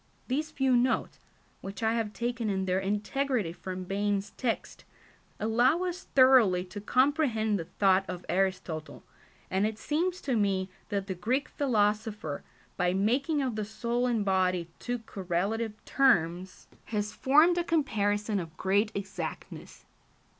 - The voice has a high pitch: Yes, high, 210 Hz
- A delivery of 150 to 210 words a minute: No, average, 140 wpm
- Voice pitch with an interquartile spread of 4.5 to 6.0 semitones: Yes, average, 4.9 semitones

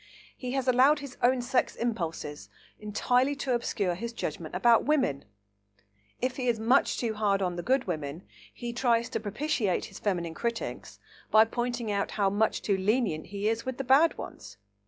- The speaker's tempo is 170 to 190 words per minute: Yes, average, 180 wpm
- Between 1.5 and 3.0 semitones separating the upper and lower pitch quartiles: No, average, 4.4 semitones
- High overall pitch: Yes, high, 230 Hz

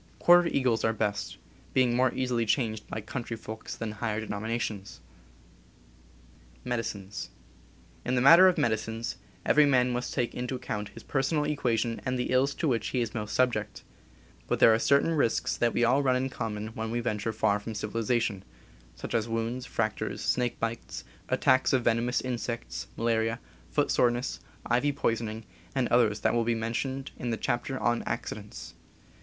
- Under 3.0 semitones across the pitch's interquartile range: Yes, narrow, 2.4 semitones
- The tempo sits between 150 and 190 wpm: Yes, average, 170 wpm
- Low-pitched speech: Yes, low, 115 Hz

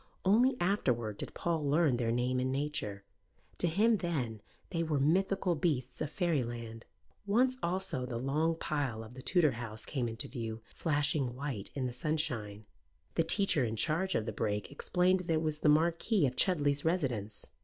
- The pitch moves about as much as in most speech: No, wide, 6.1 semitones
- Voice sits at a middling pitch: Yes, medium, 145 Hz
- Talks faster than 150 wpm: Yes, average, 175 wpm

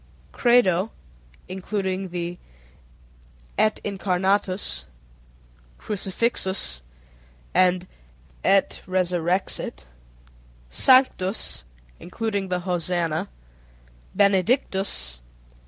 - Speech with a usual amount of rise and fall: No, narrow, 2.1 semitones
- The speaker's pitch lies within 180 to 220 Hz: Yes, medium, 185 Hz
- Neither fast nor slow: No, slow, 55 wpm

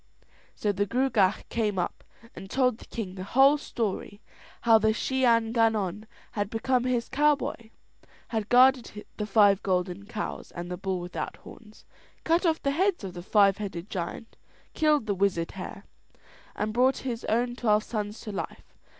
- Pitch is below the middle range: No, high, 215 Hz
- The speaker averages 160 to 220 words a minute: Yes, average, 165 wpm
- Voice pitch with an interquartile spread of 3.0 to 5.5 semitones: Yes, average, 4.0 semitones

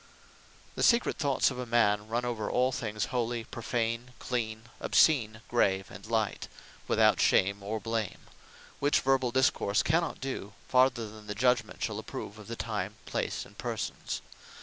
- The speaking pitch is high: No, low, 115 Hz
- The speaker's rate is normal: Yes, average, 155 wpm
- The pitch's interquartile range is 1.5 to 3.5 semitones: Yes, average, 2.8 semitones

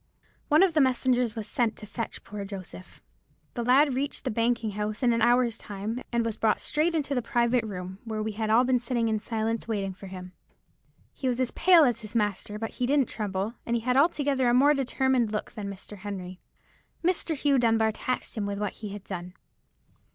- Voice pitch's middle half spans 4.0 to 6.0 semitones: No, average, 3.4 semitones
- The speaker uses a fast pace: Yes, fast, 210 wpm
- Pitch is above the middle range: Yes, high, 230 Hz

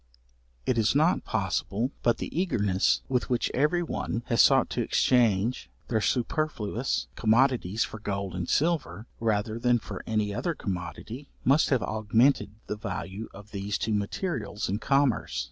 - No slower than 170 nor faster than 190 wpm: No, average, 150 wpm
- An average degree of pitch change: Yes, average, 4.2 semitones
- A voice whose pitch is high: No, low, 115 Hz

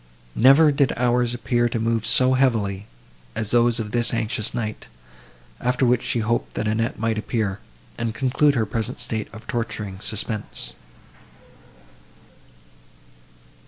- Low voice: Yes, low, 115 Hz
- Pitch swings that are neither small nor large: No, narrow, 2.1 semitones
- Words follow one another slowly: Yes, slow, 130 wpm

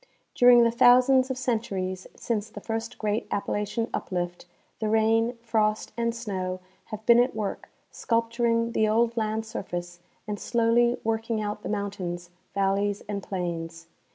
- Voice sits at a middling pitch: No, high, 220 Hz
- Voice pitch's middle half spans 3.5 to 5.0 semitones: No, average, 2.7 semitones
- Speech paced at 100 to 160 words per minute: Yes, average, 150 wpm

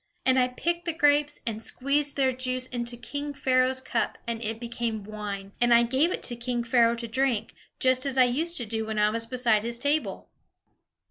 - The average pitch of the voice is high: Yes, high, 245 Hz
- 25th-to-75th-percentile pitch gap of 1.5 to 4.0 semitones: Yes, narrow, 2.6 semitones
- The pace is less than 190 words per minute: No, fast, 205 wpm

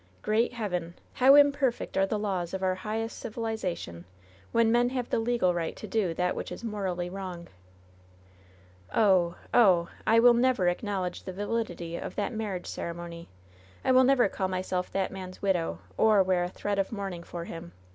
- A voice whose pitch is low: No, high, 190 Hz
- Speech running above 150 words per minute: Yes, average, 185 wpm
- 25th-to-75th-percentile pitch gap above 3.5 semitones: Yes, average, 4.2 semitones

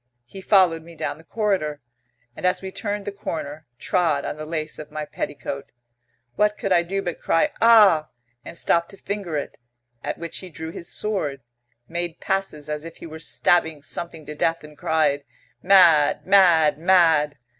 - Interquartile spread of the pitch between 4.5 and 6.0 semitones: No, average, 3.7 semitones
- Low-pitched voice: No, medium, 165 Hz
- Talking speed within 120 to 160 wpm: No, average, 175 wpm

